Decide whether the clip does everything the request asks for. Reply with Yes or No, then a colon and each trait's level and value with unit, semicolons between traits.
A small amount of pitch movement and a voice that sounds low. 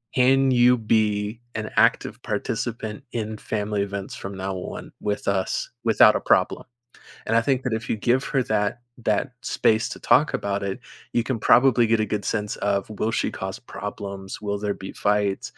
Yes: narrow, 2.2 semitones; low, 105 Hz